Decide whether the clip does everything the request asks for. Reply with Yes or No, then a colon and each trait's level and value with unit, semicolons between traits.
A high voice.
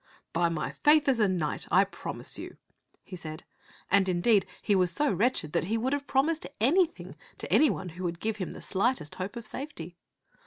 Yes: high, 200 Hz